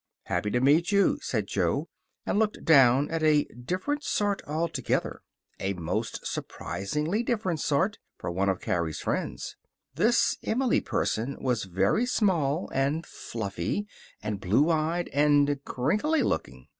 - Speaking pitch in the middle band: Yes, medium, 145 Hz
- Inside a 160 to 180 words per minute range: No, slow, 135 wpm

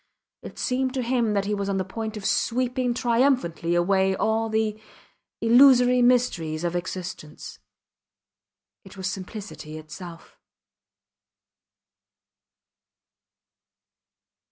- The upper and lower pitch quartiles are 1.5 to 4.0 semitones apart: No, average, 5.0 semitones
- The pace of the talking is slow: Yes, slow, 95 wpm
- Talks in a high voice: Yes, high, 210 Hz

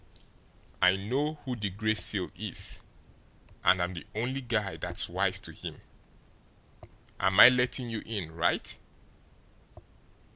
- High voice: No, low, 110 Hz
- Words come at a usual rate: No, slow, 130 wpm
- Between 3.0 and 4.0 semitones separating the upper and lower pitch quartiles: No, average, 4.8 semitones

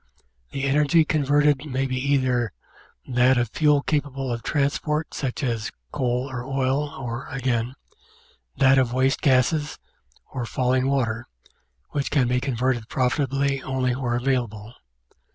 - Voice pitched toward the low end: Yes, low, 130 Hz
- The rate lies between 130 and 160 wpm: Yes, slow, 135 wpm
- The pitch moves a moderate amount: No, narrow, 2.1 semitones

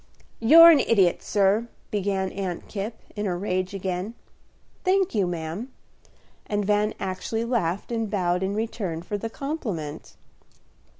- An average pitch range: Yes, average, 3.5 semitones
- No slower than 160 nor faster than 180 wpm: No, slow, 135 wpm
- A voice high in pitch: Yes, high, 200 Hz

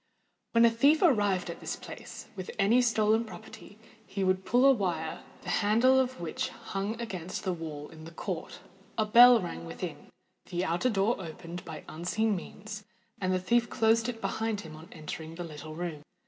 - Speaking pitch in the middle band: No, high, 200 Hz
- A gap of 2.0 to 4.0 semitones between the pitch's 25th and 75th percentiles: No, average, 5.2 semitones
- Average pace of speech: Yes, average, 175 wpm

